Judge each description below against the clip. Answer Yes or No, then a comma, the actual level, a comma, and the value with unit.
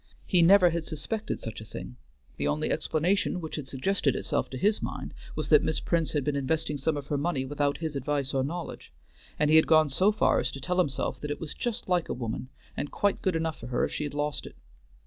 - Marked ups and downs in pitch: No, average, 3.8 semitones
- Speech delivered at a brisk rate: Yes, fast, 245 wpm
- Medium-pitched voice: Yes, medium, 150 Hz